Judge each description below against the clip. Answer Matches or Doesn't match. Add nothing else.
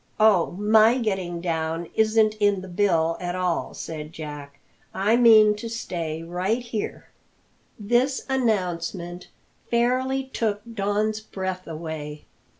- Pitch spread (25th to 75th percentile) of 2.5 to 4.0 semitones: Doesn't match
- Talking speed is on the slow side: Matches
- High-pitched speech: Matches